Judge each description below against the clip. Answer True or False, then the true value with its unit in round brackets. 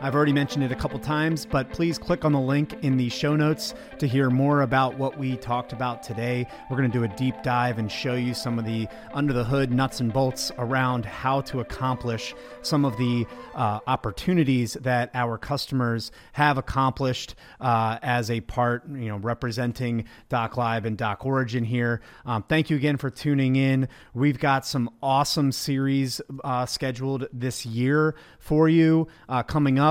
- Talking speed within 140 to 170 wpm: False (185 wpm)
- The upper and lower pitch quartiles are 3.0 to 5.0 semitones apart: False (2.6 semitones)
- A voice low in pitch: True (130 Hz)